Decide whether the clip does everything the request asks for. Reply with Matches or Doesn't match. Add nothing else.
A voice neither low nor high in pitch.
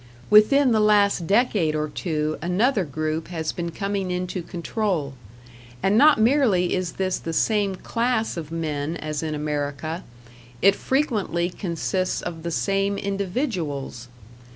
Matches